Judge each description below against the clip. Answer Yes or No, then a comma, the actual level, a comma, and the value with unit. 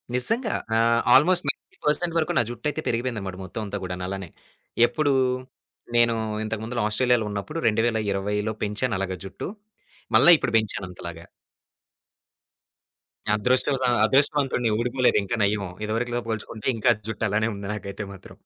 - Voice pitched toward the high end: No, low, 110 Hz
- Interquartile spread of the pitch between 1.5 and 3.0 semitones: No, average, 3.7 semitones